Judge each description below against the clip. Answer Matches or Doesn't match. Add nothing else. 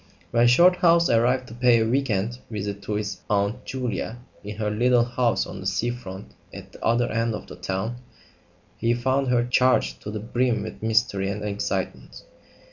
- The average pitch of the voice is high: Doesn't match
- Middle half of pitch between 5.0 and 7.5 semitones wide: Doesn't match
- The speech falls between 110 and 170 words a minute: Doesn't match